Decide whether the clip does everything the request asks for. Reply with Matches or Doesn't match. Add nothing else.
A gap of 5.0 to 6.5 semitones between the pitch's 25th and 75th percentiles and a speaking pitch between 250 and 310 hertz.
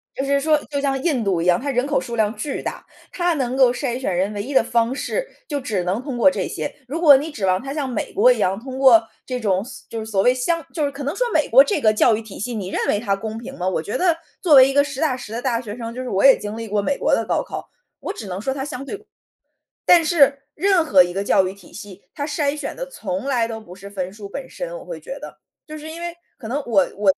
Matches